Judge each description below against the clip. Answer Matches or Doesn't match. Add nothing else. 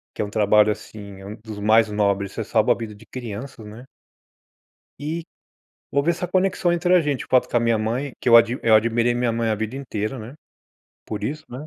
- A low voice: Matches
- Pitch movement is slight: Doesn't match